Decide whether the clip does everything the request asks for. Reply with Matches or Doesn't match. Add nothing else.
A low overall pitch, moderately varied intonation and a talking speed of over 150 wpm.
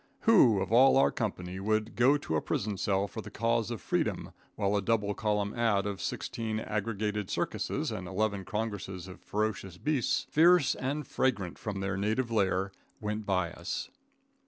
Matches